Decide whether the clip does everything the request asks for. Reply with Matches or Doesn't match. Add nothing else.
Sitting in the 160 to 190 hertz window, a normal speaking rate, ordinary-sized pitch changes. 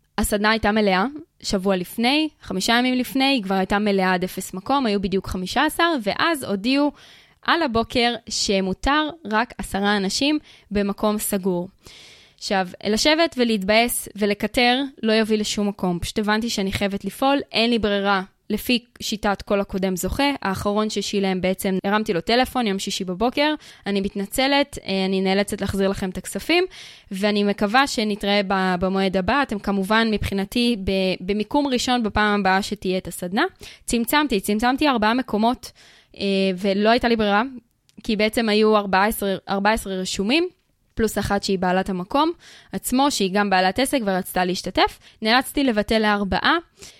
Doesn't match